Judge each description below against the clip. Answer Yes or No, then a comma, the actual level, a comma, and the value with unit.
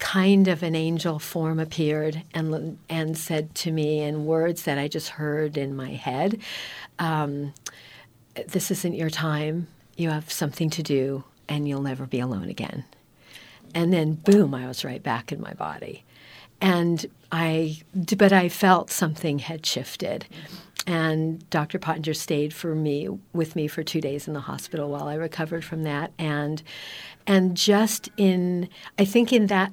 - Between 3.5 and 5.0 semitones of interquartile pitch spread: No, average, 2.7 semitones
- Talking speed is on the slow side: No, average, 165 wpm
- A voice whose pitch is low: No, medium, 160 Hz